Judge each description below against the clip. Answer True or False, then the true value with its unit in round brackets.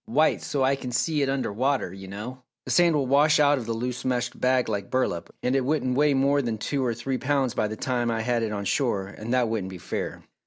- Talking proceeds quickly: True (260 wpm)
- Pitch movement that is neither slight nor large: True (3.5 semitones)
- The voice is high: False (125 Hz)